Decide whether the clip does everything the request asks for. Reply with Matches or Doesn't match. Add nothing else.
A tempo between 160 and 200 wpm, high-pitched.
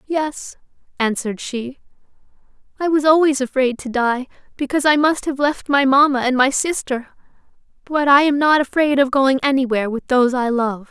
Matches